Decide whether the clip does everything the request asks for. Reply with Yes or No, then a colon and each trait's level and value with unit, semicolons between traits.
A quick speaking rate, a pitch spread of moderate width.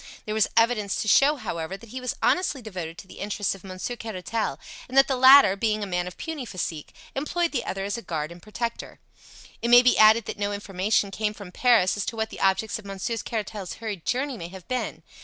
Yes: fast, 230 wpm; average, 4.1 semitones